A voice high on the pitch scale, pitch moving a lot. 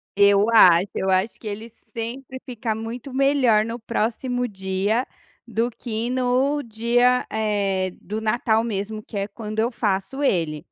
No: high, 225 Hz; average, 3.2 semitones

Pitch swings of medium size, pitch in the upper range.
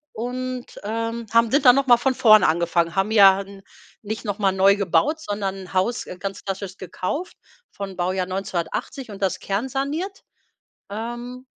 Yes: average, 4.2 semitones; high, 205 Hz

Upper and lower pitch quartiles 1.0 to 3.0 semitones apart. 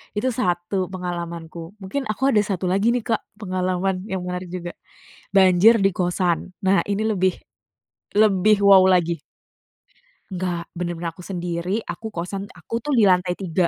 Yes: narrow, 2.4 semitones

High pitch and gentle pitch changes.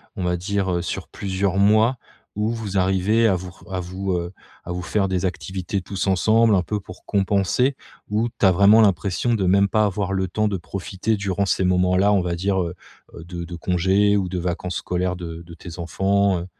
No: very low, 95 Hz; narrow, 2.1 semitones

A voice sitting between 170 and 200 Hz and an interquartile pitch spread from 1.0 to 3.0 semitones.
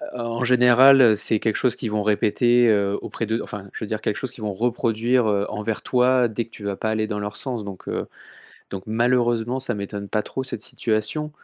No: low, 110 Hz; average, 2.7 semitones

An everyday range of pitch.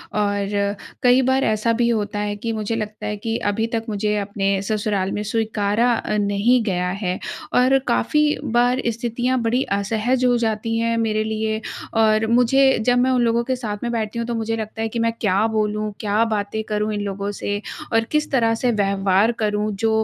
No: narrow, 2.1 semitones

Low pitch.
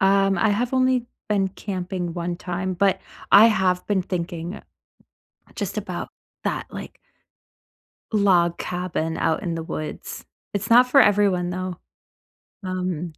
No: medium, 185 Hz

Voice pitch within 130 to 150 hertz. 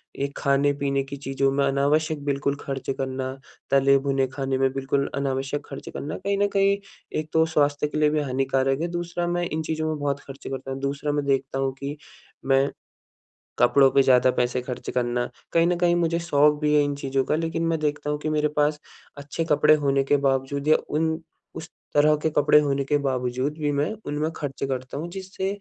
Yes: medium, 140 Hz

